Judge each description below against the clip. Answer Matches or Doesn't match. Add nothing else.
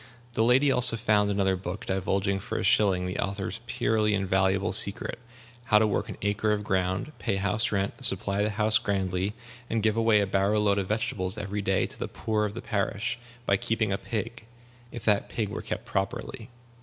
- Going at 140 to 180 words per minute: Doesn't match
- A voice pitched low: Matches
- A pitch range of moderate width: Doesn't match